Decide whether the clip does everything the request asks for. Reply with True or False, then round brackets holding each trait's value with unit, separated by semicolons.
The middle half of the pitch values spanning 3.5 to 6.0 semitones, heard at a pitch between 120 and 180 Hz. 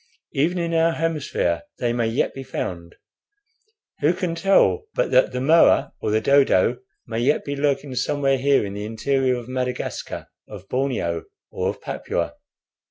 True (4.7 semitones; 135 Hz)